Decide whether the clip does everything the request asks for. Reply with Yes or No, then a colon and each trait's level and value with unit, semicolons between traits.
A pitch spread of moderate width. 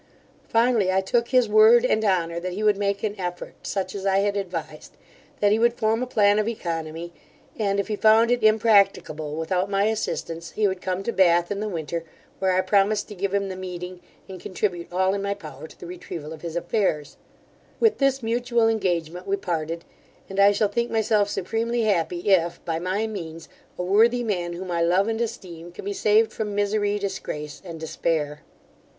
Yes: average, 3.8 semitones